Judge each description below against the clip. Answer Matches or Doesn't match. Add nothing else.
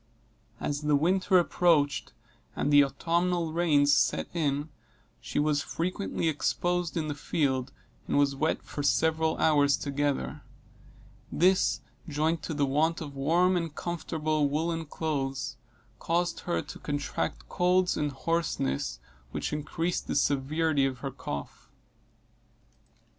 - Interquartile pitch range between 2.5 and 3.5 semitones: Matches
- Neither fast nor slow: Doesn't match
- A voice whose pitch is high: Doesn't match